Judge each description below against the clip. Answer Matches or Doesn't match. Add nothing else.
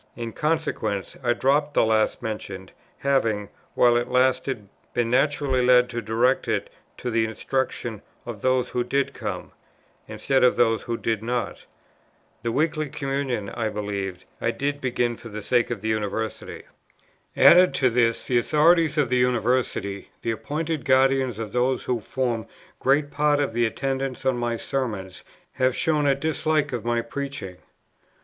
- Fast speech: Doesn't match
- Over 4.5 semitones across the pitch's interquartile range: Doesn't match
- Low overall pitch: Matches